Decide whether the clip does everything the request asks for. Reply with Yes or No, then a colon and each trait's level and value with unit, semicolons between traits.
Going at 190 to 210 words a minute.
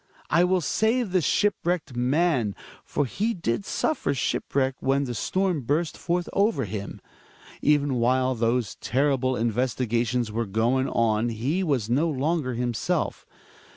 No: average, 140 wpm